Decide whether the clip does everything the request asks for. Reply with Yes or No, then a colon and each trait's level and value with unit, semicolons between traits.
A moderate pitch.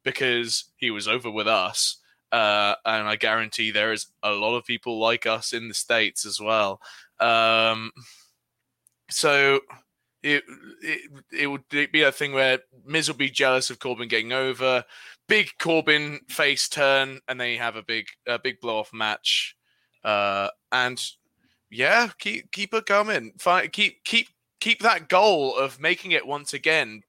No: low, 130 Hz